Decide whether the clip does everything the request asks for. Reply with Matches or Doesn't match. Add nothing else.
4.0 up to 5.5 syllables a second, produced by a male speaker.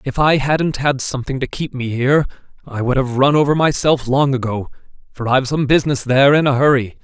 Doesn't match